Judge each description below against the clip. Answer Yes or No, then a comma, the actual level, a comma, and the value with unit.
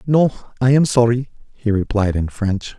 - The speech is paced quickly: No, average, 170 wpm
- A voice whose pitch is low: Yes, low, 115 Hz